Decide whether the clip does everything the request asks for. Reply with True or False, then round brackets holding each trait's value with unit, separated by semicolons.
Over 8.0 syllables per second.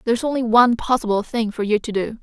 False (6.7 syllables/s)